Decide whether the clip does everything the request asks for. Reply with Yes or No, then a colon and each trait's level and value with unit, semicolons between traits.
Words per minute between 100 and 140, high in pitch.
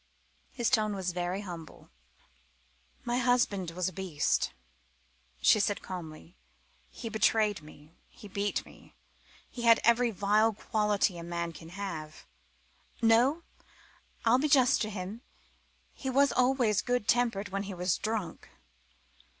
Yes: slow, 135 wpm; high, 205 Hz